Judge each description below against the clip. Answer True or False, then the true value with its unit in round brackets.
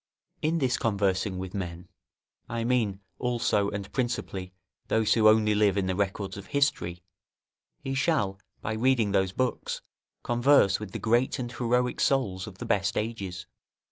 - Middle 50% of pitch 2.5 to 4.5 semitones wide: True (4.1 semitones)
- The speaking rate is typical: True (155 wpm)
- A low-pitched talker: True (105 Hz)